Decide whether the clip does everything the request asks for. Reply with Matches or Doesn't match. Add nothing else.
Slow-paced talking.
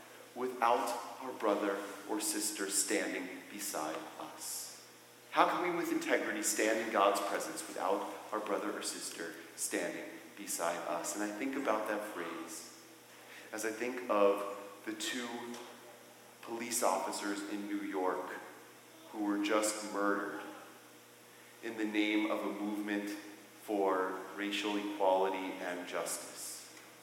Matches